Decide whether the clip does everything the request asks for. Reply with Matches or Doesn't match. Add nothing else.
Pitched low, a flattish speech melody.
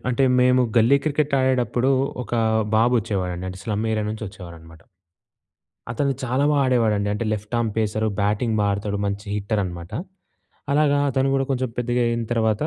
Doesn't match